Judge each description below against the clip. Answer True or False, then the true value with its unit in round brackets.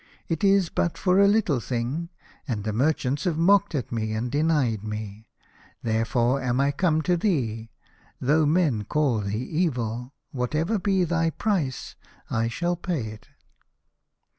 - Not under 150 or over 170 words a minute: True (160 wpm)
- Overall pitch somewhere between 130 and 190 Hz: True (140 Hz)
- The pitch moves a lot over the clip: True (6.8 semitones)